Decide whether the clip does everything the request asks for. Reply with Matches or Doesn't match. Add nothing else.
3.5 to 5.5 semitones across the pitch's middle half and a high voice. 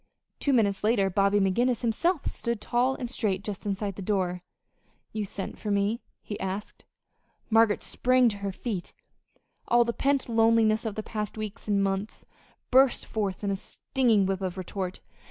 Doesn't match